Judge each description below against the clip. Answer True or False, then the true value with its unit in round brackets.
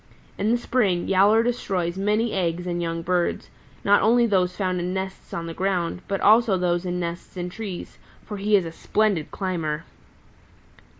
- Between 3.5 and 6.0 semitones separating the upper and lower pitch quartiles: False (3.1 semitones)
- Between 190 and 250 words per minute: False (175 wpm)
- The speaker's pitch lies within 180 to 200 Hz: True (185 Hz)